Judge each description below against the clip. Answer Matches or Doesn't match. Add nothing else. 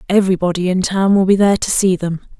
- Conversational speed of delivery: Doesn't match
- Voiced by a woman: Matches